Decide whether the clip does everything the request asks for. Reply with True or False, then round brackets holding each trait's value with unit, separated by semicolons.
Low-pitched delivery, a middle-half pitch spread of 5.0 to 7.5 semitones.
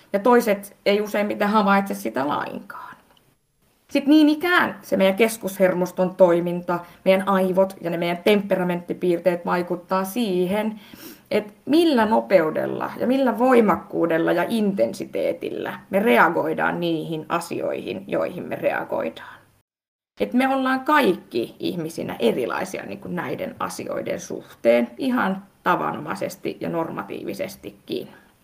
False (195 Hz; 5.5 semitones)